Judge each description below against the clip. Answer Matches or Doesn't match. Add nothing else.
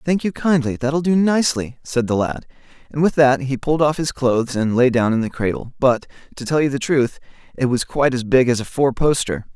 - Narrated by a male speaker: Matches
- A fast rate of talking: Matches